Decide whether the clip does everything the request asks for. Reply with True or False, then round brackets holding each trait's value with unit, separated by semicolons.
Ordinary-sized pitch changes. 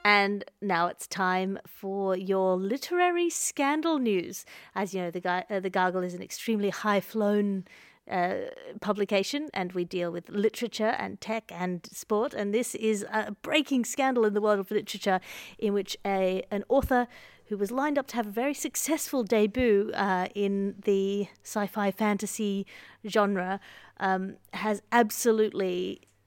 True (3.2 semitones)